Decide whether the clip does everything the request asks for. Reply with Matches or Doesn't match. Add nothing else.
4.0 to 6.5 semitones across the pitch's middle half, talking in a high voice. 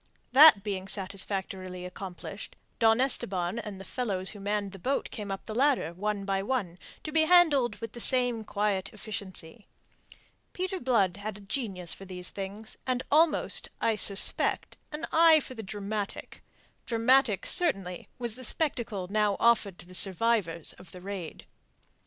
Matches